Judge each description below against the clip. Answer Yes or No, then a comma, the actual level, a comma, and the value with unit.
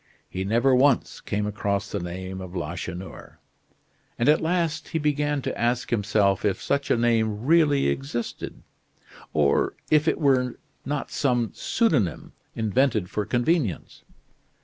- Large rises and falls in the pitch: Yes, wide, 6.1 semitones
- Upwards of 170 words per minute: No, slow, 135 wpm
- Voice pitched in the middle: No, low, 120 Hz